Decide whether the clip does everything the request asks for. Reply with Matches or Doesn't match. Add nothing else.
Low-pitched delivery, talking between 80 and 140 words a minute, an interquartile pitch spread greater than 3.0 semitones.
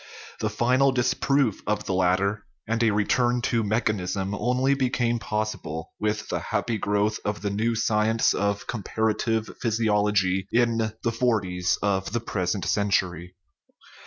Doesn't match